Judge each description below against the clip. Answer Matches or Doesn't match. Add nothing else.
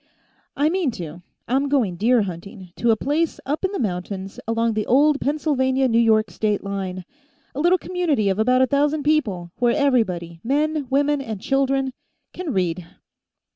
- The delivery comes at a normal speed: Matches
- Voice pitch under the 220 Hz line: Doesn't match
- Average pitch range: Doesn't match